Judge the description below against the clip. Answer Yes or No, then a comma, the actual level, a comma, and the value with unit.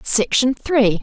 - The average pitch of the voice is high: Yes, high, 240 Hz